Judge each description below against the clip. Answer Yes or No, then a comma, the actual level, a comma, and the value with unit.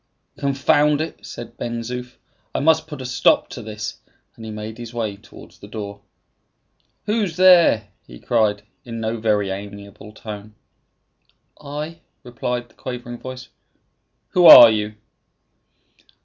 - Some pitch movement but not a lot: Yes, average, 4.4 semitones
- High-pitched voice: No, low, 115 Hz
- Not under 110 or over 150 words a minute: Yes, slow, 135 wpm